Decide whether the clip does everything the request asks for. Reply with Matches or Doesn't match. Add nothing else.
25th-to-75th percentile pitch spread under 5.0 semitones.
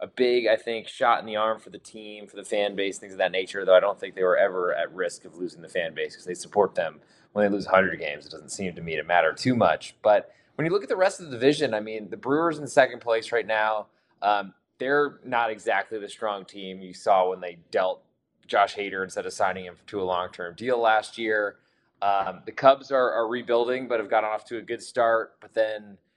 Matches